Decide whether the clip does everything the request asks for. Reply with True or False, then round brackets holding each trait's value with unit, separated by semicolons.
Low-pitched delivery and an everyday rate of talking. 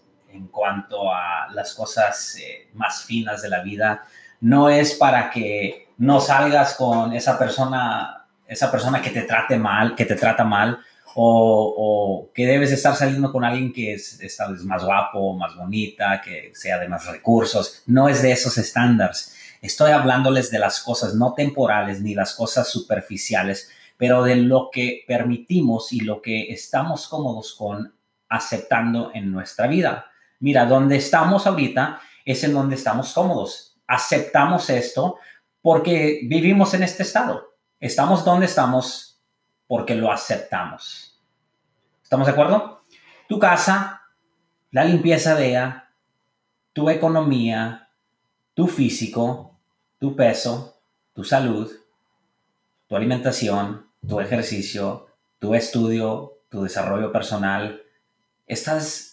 False (125 Hz; 130 wpm)